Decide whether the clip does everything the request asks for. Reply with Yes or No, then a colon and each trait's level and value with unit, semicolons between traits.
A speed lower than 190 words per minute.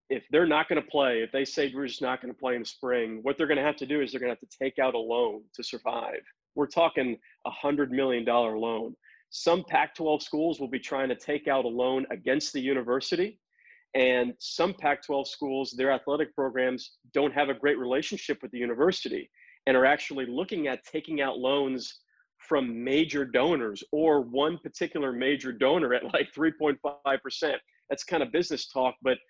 No: fast, 205 wpm